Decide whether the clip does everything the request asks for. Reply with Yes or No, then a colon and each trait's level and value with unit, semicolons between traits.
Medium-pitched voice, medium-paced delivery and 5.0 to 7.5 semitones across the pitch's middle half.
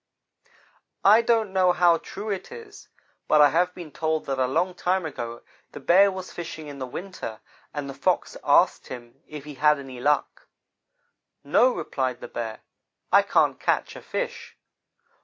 Yes: medium, 160 Hz; average, 170 wpm; wide, 5.5 semitones